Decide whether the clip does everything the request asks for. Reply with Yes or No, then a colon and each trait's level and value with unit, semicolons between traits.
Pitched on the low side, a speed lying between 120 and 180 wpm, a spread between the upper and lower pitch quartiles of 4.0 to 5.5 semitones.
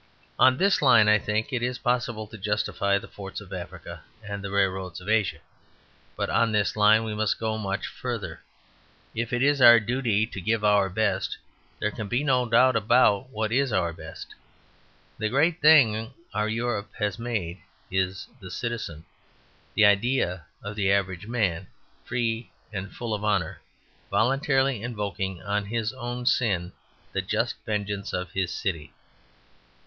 No: low, 105 Hz; average, 160 wpm; average, 3.4 semitones